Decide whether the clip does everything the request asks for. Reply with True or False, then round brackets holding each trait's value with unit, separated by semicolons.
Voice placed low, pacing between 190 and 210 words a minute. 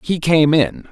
False (150 Hz; 200 wpm)